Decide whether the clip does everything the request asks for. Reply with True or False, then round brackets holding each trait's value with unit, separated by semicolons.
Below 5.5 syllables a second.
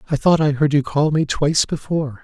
False (6.0 syllables/s)